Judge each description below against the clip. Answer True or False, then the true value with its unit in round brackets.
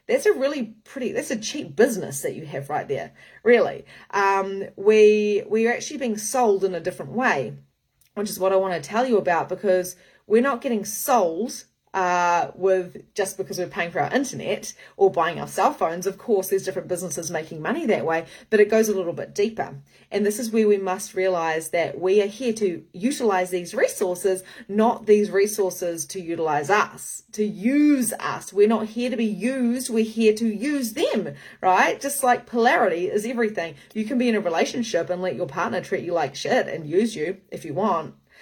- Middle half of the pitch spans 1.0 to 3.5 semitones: False (4.3 semitones)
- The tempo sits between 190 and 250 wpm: True (200 wpm)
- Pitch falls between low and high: False (205 Hz)